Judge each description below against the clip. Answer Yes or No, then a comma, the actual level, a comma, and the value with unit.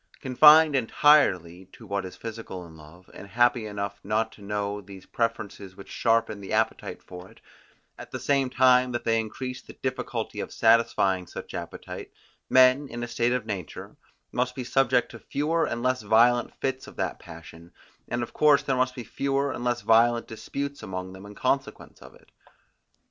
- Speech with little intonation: No, average, 4.2 semitones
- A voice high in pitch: No, low, 115 Hz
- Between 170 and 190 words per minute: Yes, average, 180 wpm